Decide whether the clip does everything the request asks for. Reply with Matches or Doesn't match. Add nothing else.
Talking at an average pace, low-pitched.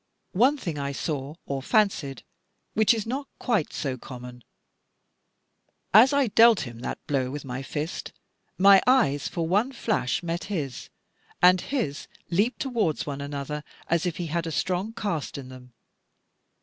Doesn't match